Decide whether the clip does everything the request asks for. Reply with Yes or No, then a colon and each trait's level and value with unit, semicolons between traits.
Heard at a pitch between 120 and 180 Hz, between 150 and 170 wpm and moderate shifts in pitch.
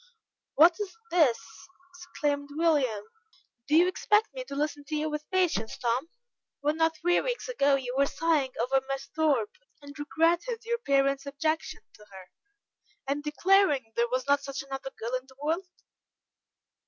No: very high, 295 Hz; average, 160 wpm; average, 3.7 semitones